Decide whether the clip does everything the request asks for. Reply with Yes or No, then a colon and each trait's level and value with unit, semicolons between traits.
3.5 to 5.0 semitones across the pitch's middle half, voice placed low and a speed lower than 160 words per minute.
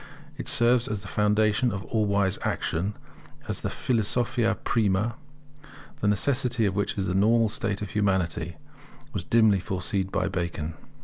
No: average, 3.0 semitones; low, 105 Hz; average, 150 wpm